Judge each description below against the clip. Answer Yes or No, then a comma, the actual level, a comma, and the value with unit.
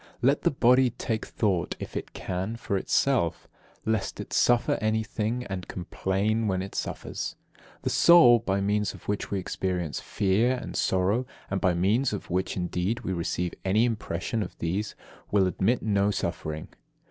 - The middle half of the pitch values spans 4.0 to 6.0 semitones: No, average, 3.6 semitones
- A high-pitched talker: No, low, 100 Hz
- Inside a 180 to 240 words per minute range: No, average, 160 wpm